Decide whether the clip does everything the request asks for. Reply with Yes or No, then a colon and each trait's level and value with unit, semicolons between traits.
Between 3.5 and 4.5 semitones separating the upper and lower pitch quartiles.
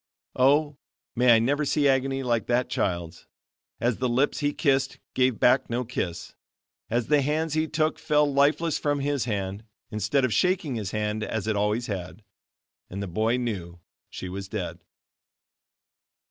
No: average, 5.2 semitones